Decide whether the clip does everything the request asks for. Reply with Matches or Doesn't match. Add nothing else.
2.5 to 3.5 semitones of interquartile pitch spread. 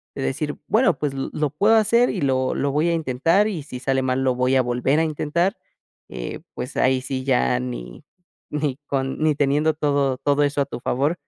Matches